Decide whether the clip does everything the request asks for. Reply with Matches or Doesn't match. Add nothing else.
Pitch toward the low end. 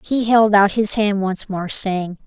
Doesn't match